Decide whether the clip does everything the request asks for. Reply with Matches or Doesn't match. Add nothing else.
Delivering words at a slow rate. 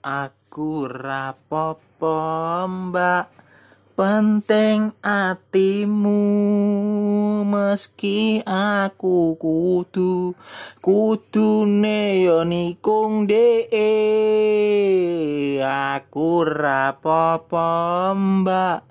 Matches